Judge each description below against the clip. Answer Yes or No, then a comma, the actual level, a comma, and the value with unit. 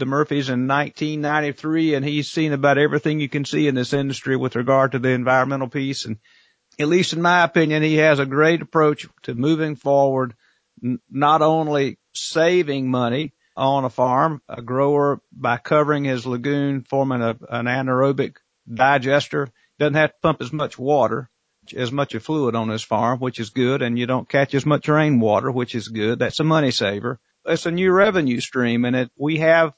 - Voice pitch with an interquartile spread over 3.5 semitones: No, average, 3.2 semitones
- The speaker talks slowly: No, average, 190 wpm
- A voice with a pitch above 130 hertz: Yes, medium, 140 Hz